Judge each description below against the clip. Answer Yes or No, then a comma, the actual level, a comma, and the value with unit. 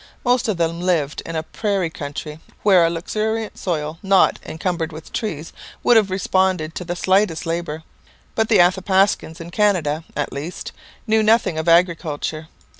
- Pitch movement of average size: Yes, average, 3.6 semitones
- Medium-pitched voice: Yes, medium, 175 Hz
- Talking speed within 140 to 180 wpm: Yes, average, 160 wpm